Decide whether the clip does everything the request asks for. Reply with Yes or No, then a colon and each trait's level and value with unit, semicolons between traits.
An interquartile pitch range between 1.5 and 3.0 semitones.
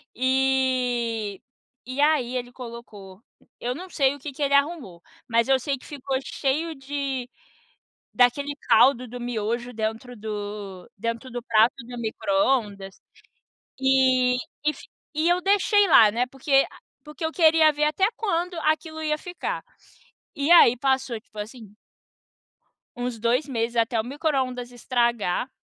No: average, 3.7 semitones